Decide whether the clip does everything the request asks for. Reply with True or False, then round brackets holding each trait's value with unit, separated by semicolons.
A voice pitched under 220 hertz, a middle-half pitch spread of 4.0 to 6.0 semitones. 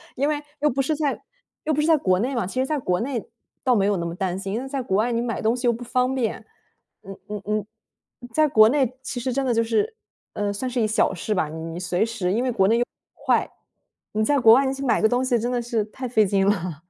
False (235 Hz; 4.3 semitones)